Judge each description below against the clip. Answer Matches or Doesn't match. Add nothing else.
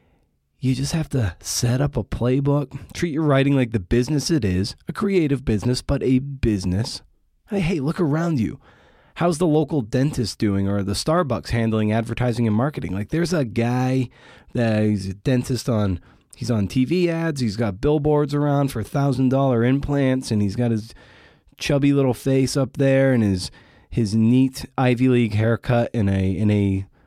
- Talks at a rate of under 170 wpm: Doesn't match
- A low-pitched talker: Matches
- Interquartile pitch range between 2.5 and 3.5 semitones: Doesn't match